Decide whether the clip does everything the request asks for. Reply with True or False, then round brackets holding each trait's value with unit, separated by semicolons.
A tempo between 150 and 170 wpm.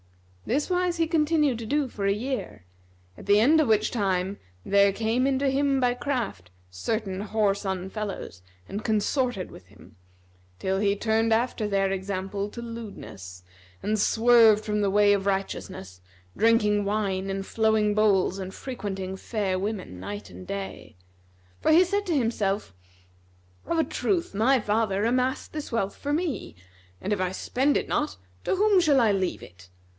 True (165 wpm)